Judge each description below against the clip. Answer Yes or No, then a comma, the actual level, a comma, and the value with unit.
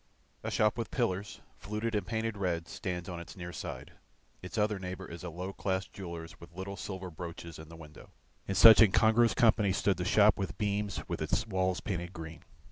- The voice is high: No, very low, 95 Hz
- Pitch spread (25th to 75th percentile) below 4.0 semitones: Yes, average, 3.3 semitones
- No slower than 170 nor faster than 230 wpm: Yes, average, 200 wpm